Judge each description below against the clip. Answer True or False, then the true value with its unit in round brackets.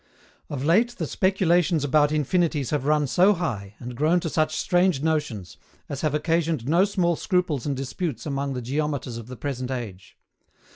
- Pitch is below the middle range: False (150 Hz)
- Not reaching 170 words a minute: False (175 wpm)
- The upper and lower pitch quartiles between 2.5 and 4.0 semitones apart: False (4.6 semitones)